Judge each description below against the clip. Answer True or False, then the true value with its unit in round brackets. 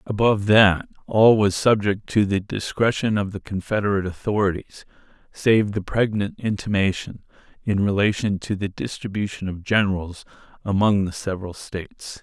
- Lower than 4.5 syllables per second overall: False (5.1 syllables/s)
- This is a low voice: True (100 Hz)